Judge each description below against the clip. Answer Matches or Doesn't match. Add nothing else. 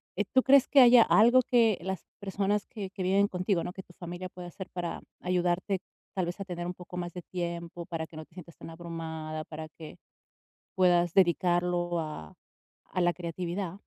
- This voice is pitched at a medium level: Matches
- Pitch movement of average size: Doesn't match